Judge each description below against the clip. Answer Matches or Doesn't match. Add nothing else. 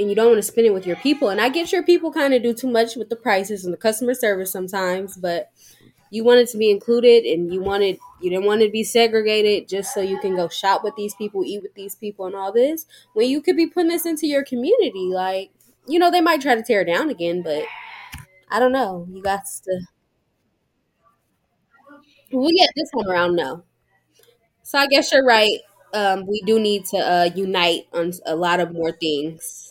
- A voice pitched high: Matches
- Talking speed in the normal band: Doesn't match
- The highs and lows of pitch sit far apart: Matches